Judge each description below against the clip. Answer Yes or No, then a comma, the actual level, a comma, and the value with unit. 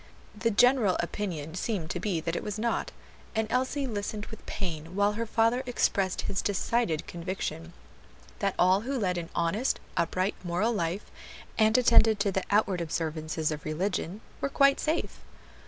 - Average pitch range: Yes, average, 4.7 semitones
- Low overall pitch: No, high, 200 Hz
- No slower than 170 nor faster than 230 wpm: No, average, 160 wpm